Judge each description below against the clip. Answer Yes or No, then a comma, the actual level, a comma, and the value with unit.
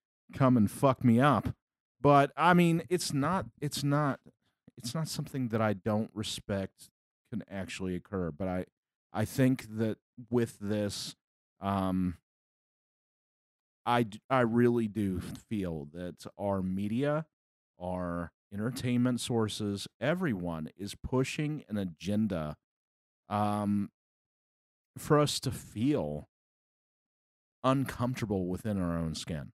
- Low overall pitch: Yes, low, 105 Hz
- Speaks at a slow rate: Yes, slow, 115 wpm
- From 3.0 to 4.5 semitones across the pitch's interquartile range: No, wide, 5.6 semitones